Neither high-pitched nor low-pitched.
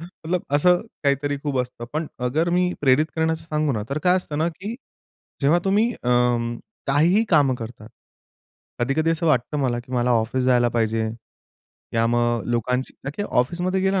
Yes: medium, 145 Hz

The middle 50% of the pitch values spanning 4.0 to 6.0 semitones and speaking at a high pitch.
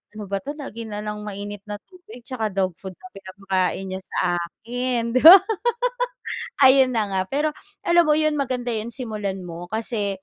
Yes: average, 4.6 semitones; high, 220 Hz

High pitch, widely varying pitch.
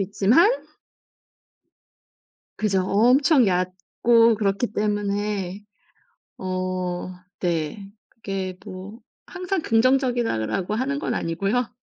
No: high, 205 Hz; average, 4.3 semitones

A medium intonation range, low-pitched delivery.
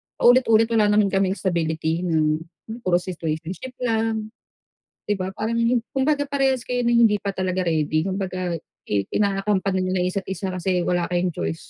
No: average, 3.9 semitones; high, 190 Hz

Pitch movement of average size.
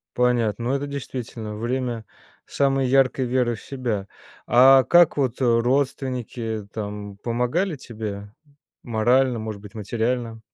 Yes: average, 3.0 semitones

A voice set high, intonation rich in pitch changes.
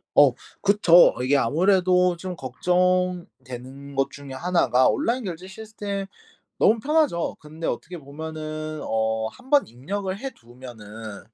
No: medium, 165 Hz; wide, 6.2 semitones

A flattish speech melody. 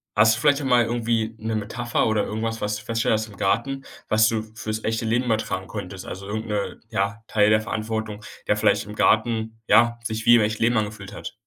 Yes: narrow, 1.4 semitones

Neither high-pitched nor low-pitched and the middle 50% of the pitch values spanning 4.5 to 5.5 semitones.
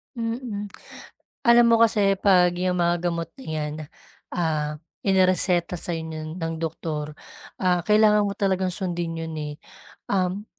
No: medium, 180 Hz; average, 3.6 semitones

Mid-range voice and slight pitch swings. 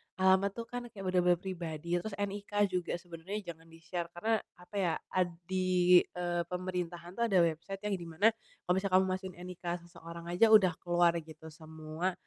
Yes: medium, 180 Hz; narrow, 2.0 semitones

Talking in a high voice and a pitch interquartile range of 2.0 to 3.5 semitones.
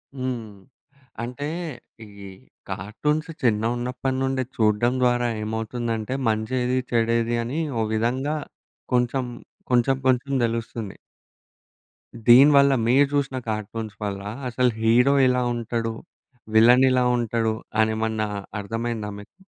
No: low, 120 Hz; narrow, 2.4 semitones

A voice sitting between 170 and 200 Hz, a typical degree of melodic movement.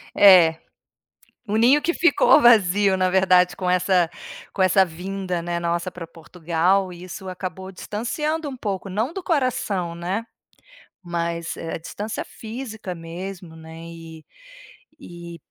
Yes: medium, 185 Hz; average, 3.4 semitones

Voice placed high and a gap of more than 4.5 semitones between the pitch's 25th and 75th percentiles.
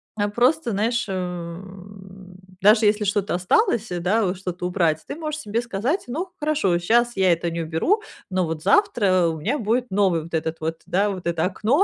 Yes: high, 195 Hz; average, 5.1 semitones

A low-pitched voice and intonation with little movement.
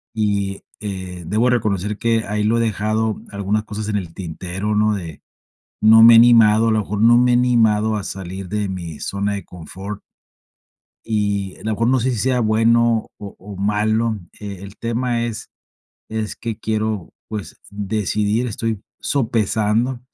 Yes: low, 105 Hz; narrow, 2.2 semitones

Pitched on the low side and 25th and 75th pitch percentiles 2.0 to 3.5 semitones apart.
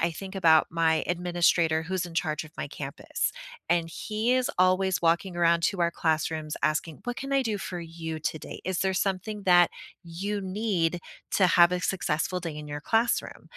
No: medium, 175 Hz; average, 2.8 semitones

